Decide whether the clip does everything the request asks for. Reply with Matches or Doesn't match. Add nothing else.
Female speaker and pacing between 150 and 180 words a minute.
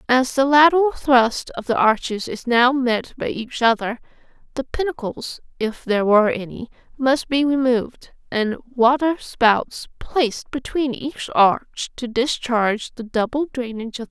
Matches